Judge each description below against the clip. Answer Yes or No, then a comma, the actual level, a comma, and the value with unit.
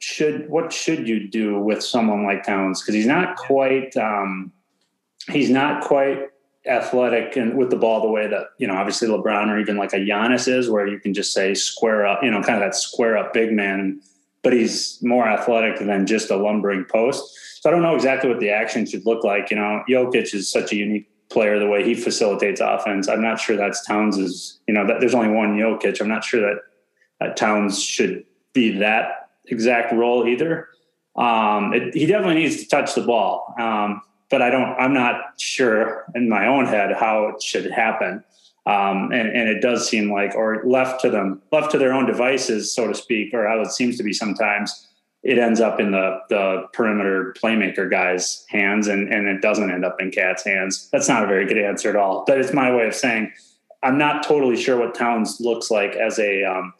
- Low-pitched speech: Yes, low, 110 Hz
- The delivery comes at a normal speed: No, fast, 215 wpm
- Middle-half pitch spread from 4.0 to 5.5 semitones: No, average, 3.2 semitones